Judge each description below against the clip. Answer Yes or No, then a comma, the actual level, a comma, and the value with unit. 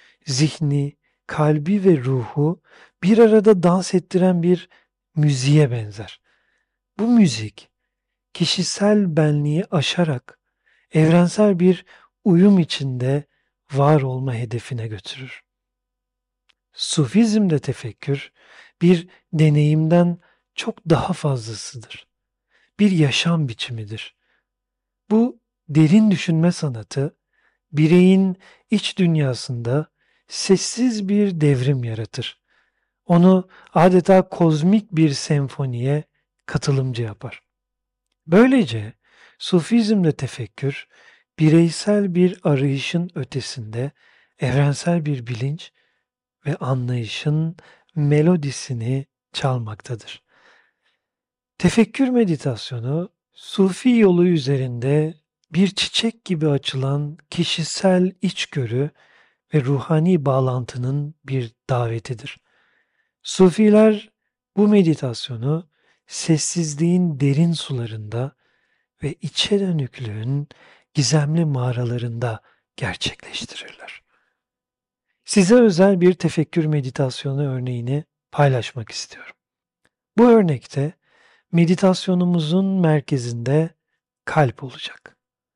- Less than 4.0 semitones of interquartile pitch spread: No, wide, 5.4 semitones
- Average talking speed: No, slow, 75 wpm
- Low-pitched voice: No, medium, 155 Hz